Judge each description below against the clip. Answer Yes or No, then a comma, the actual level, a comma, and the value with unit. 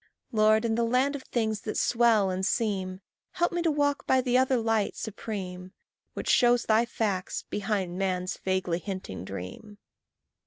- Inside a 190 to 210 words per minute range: No, average, 160 wpm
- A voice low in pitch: No, high, 215 Hz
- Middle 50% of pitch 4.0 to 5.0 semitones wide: Yes, average, 4.3 semitones